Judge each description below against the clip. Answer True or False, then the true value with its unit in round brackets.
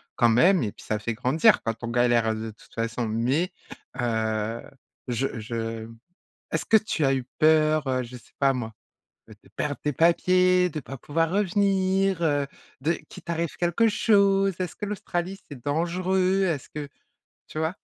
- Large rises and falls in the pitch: True (7.3 semitones)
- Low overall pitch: False (150 Hz)